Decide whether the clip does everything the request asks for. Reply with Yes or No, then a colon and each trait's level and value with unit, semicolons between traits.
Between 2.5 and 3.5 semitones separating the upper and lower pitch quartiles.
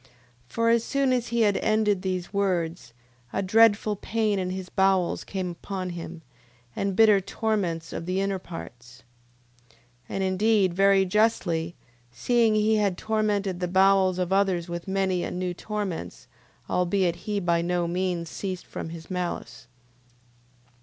Yes: average, 2.9 semitones